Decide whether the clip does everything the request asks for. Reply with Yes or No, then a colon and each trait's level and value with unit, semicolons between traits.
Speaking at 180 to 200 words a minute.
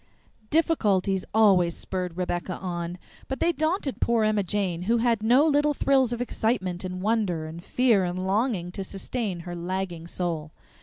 No: average, 160 wpm